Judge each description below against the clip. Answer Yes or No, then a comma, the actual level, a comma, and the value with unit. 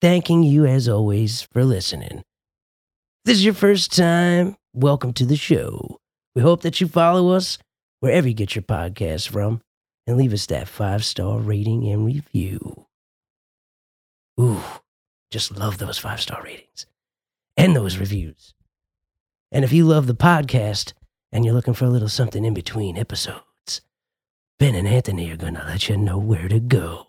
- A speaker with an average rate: Yes, average, 165 wpm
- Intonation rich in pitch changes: Yes, wide, 5.9 semitones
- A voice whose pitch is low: Yes, low, 115 Hz